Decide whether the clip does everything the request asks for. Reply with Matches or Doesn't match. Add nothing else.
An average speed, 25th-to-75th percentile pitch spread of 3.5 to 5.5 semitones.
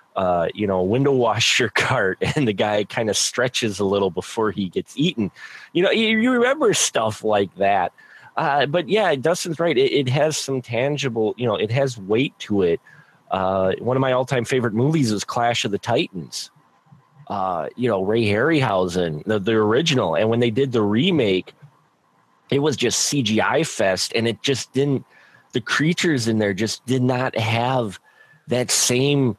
Matches